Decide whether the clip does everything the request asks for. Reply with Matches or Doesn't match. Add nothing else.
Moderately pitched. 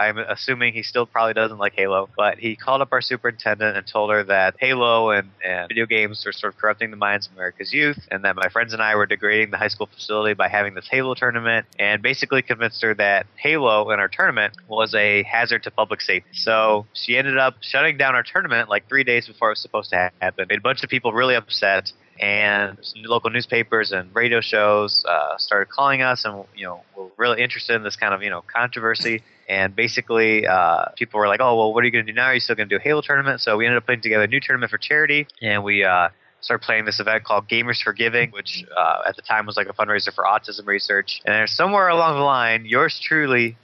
Doesn't match